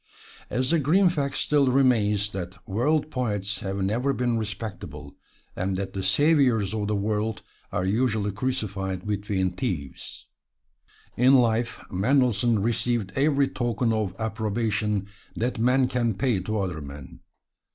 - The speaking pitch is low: Yes, low, 110 Hz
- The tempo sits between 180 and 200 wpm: No, slow, 135 wpm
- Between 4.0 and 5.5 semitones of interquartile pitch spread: Yes, average, 4.4 semitones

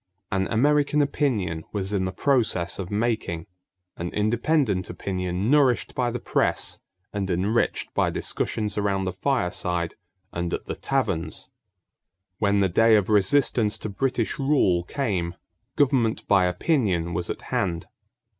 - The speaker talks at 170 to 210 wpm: No, slow, 135 wpm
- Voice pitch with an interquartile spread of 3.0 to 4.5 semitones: No, average, 5.1 semitones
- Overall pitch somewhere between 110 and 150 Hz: No, low, 100 Hz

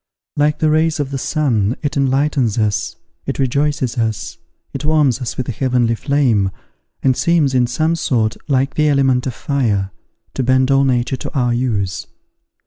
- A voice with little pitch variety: No, average, 3.2 semitones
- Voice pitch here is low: Yes, low, 130 Hz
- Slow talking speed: No, average, 170 wpm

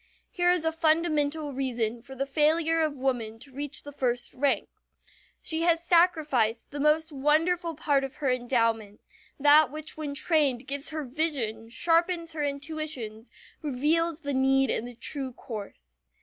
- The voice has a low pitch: No, very high, 285 Hz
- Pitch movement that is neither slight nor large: Yes, average, 3.9 semitones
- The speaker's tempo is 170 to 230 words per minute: No, average, 155 wpm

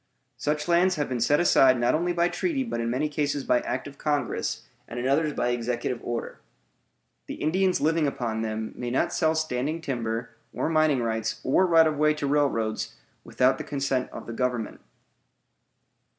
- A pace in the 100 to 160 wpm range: No, average, 180 wpm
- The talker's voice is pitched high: No, medium, 140 Hz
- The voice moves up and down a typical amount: Yes, average, 4.4 semitones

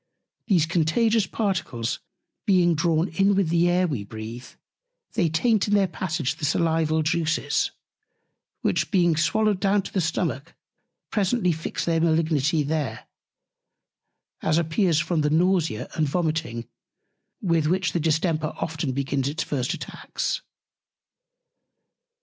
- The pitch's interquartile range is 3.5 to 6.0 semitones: No, average, 3.0 semitones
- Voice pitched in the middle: Yes, medium, 165 Hz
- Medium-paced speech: No, slow, 125 wpm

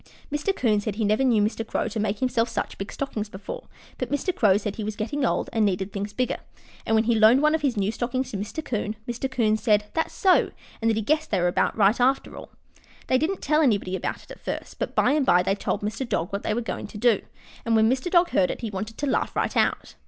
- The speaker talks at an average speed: No, fast, 265 wpm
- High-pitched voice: Yes, high, 225 Hz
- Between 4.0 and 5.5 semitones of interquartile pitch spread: Yes, average, 4.3 semitones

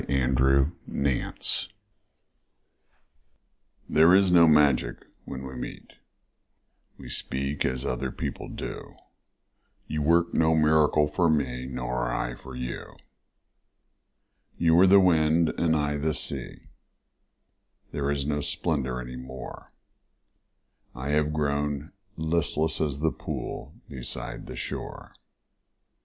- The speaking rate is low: Yes, slow, 115 wpm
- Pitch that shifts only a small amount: No, average, 3.3 semitones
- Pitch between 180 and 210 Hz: No, very low, 75 Hz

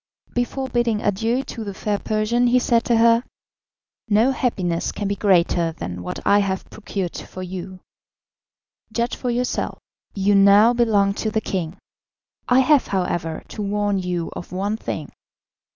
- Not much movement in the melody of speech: No, average, 3.8 semitones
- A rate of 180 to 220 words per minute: No, average, 155 wpm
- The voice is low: No, high, 205 Hz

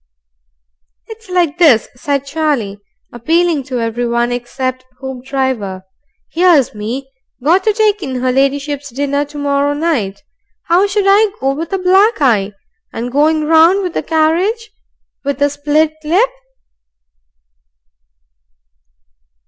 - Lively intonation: No, average, 5.0 semitones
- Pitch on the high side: Yes, very high, 285 Hz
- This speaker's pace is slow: Yes, slow, 125 wpm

